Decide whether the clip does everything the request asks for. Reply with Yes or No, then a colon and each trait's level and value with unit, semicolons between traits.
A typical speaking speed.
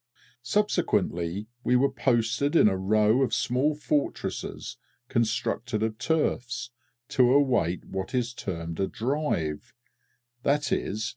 No: slow, 115 wpm